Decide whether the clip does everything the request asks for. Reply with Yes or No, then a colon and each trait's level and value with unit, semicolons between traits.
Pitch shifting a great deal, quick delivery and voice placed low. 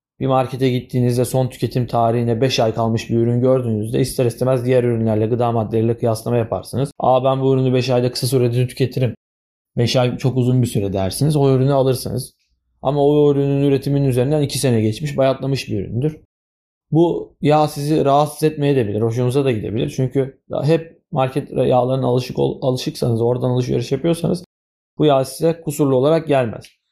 No: average, 2.9 semitones; fast, 165 wpm; low, 130 Hz